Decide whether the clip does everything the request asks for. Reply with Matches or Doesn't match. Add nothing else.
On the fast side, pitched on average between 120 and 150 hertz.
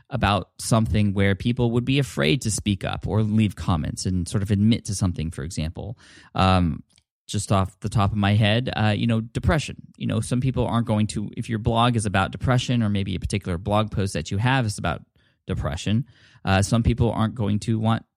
Doesn't match